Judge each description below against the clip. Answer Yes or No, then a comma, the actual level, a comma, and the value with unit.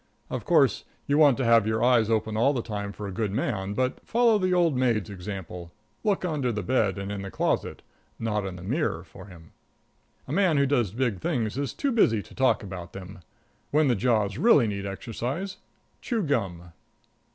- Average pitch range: No, wide, 6.0 semitones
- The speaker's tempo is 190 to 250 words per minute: Yes, average, 195 wpm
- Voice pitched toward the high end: No, low, 115 Hz